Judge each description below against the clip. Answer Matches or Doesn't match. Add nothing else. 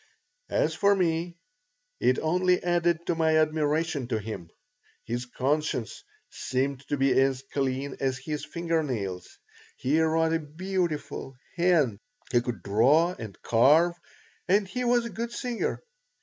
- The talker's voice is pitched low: Doesn't match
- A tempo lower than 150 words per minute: Matches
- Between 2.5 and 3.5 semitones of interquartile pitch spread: Doesn't match